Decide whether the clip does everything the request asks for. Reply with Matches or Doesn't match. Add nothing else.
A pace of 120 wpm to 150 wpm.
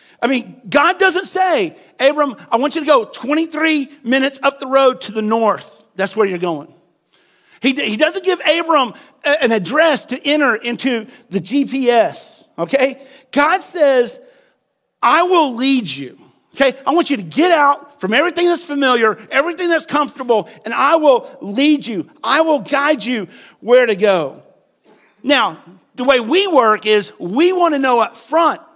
Doesn't match